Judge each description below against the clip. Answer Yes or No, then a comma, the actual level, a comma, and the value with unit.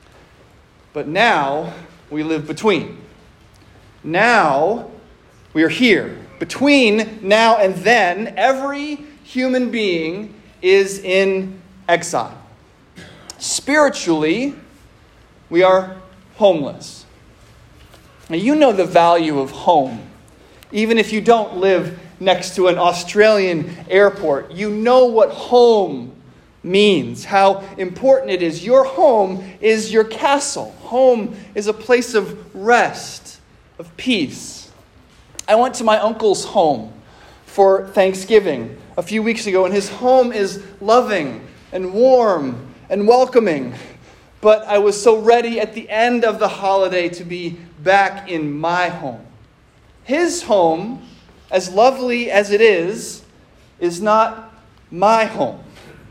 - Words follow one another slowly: Yes, slow, 120 wpm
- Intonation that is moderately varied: Yes, average, 4.4 semitones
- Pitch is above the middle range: Yes, high, 210 Hz